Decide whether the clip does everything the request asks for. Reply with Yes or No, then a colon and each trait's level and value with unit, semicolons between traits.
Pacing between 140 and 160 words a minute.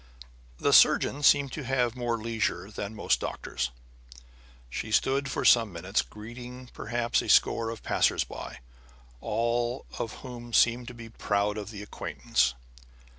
Yes: average, 145 wpm